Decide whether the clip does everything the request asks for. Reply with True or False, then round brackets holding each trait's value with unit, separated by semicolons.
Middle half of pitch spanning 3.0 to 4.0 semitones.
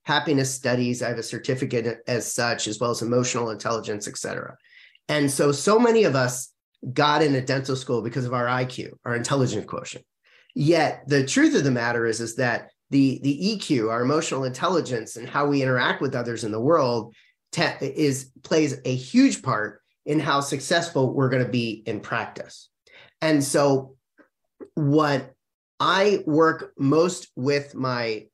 True (3.6 semitones)